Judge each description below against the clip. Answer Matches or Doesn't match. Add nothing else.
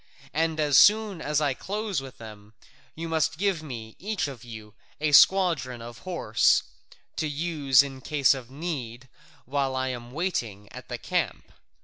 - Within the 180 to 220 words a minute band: Doesn't match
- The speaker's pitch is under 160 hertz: Matches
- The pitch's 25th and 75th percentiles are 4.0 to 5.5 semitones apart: Matches